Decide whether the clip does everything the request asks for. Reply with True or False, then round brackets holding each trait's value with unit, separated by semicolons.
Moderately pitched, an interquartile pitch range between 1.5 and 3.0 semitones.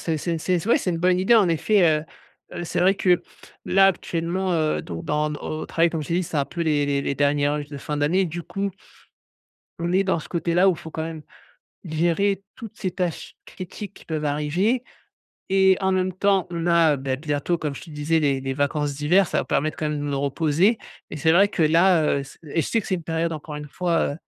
False (165 Hz; 3.6 semitones)